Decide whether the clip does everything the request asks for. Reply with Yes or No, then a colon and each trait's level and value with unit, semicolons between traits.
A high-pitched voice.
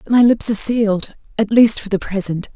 Yes: high, 210 Hz